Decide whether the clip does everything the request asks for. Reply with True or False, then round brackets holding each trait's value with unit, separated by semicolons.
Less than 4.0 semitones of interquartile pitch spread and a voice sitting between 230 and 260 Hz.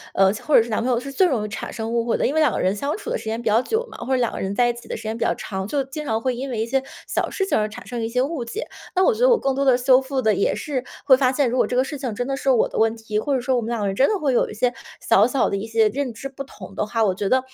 True (3.5 semitones; 245 Hz)